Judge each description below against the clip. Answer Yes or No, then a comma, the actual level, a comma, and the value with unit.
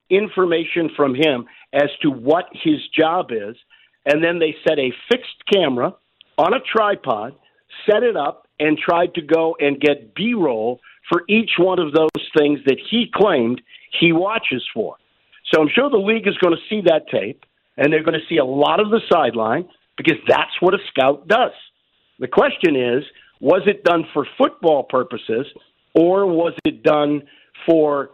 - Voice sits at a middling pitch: Yes, medium, 165 Hz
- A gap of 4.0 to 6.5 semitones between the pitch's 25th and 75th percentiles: Yes, average, 4.4 semitones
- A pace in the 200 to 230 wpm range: No, average, 175 wpm